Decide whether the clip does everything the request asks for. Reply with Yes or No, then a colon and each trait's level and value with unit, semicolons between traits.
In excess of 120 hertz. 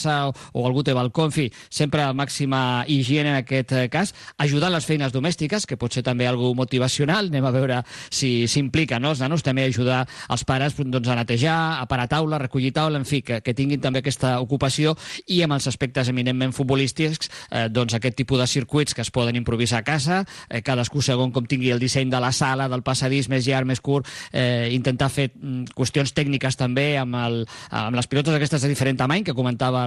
Yes: low, 135 Hz